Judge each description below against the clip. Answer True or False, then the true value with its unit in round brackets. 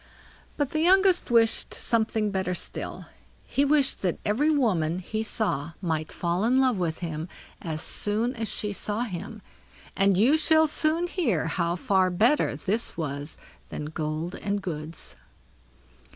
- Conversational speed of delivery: True (150 wpm)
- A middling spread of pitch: False (6.9 semitones)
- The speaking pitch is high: True (205 Hz)